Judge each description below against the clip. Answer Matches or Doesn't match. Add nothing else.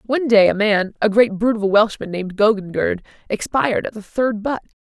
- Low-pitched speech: Doesn't match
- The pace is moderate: Doesn't match